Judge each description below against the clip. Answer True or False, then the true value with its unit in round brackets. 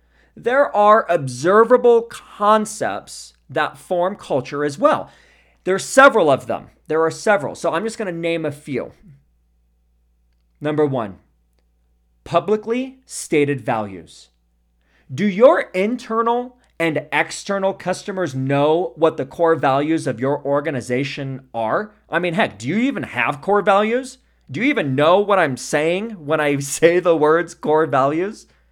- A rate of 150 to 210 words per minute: False (140 wpm)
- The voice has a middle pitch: True (155 Hz)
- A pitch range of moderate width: False (7.9 semitones)